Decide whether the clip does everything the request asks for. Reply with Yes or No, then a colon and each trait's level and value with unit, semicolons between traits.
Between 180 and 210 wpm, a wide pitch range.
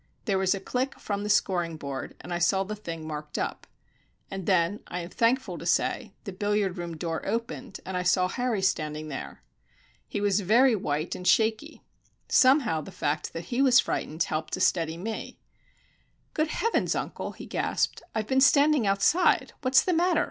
Yes: average, 185 wpm; wide, 5.7 semitones